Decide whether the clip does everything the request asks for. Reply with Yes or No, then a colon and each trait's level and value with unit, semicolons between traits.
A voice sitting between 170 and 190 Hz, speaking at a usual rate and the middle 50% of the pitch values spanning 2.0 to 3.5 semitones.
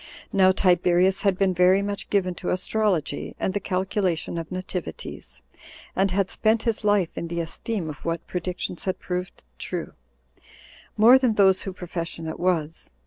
Yes: medium, 185 Hz; average, 165 wpm; narrow, 2.5 semitones